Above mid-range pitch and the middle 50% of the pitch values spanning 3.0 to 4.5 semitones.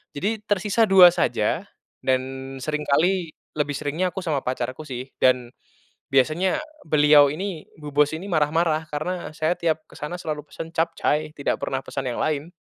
No: medium, 155 Hz; average, 3.3 semitones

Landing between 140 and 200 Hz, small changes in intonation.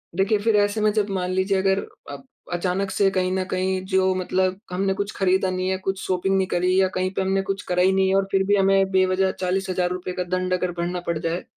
Yes: high, 190 Hz; narrow, 1.0 semitones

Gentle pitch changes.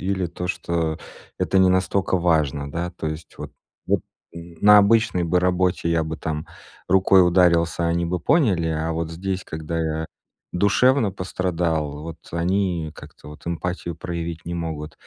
Yes: narrow, 2.2 semitones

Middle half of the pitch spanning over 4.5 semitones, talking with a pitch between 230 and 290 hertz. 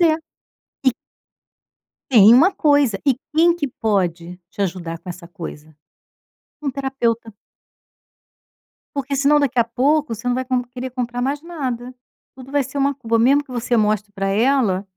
Yes: average, 4.9 semitones; high, 245 Hz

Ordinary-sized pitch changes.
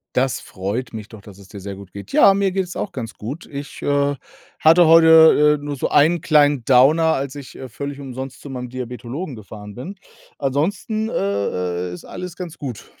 No: wide, 6.3 semitones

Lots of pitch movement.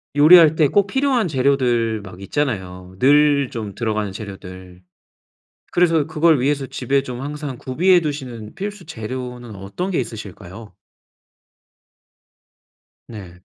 Yes: wide, 6.0 semitones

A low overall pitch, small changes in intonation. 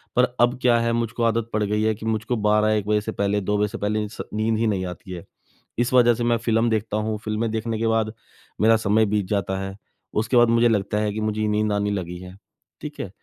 Yes: low, 110 Hz; narrow, 1.7 semitones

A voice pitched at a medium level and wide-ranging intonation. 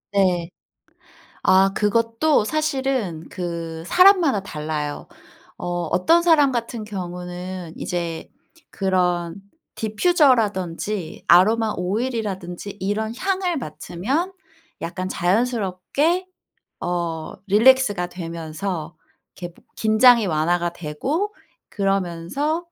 No: high, 195 Hz; wide, 6.2 semitones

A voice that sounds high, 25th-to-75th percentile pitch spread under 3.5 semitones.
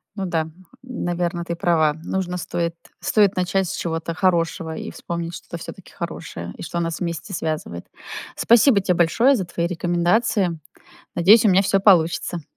No: medium, 175 Hz; narrow, 2.4 semitones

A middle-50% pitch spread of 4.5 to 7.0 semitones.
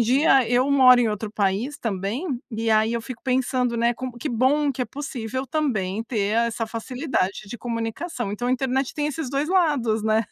No: average, 3.3 semitones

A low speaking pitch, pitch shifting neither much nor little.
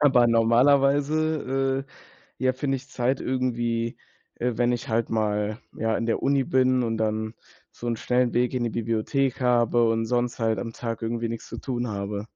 No: low, 120 Hz; narrow, 2.3 semitones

